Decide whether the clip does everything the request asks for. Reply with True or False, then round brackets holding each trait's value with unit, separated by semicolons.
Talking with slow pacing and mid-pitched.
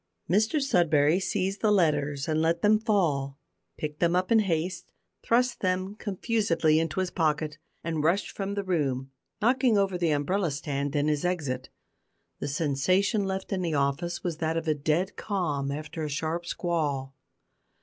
False (165 wpm; 165 Hz)